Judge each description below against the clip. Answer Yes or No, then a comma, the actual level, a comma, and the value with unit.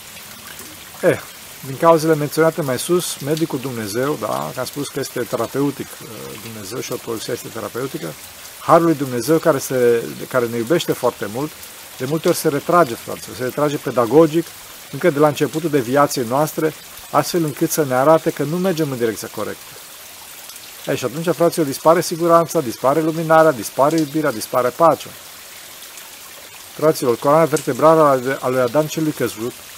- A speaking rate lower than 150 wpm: No, average, 160 wpm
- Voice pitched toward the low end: No, medium, 150 Hz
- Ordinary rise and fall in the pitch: Yes, average, 4.1 semitones